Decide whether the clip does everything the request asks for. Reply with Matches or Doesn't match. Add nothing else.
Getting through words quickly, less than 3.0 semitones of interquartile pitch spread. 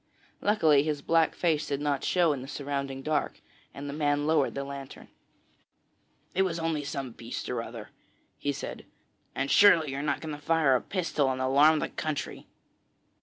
Doesn't match